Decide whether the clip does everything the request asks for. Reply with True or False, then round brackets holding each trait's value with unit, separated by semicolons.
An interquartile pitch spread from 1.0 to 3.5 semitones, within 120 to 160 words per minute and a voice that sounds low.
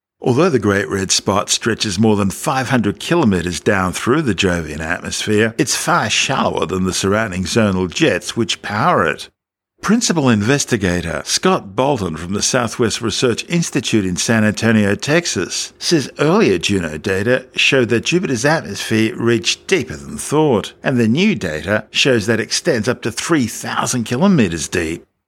False (5.6 semitones; 150 wpm; 110 Hz)